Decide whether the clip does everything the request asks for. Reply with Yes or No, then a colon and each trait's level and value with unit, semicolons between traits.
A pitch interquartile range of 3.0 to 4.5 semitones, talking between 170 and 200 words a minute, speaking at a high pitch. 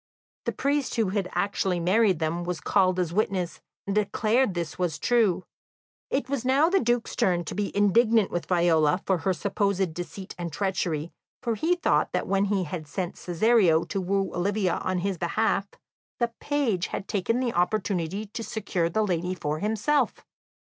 Yes: average, 3.8 semitones; average, 175 wpm; high, 195 Hz